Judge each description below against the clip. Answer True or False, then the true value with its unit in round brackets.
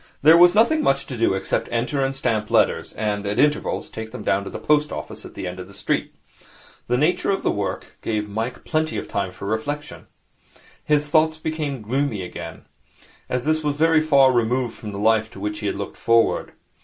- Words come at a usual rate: False (210 wpm)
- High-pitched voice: False (125 Hz)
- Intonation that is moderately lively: False (6.1 semitones)